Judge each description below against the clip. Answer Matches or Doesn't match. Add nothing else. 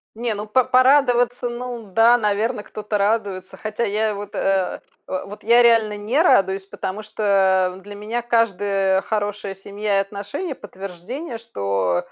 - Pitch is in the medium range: Doesn't match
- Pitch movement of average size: Matches